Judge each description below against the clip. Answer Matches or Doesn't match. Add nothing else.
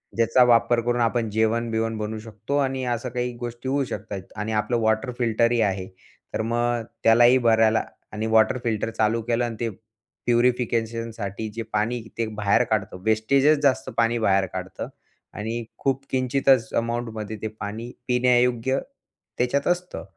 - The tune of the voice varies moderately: Doesn't match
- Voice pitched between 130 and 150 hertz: Doesn't match